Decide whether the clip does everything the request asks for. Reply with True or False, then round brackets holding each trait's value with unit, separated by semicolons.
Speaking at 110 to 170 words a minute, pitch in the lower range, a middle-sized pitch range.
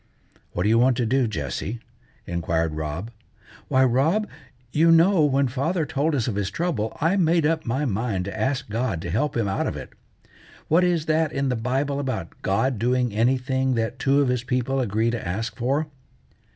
False (190 wpm; 125 Hz; 4.6 semitones)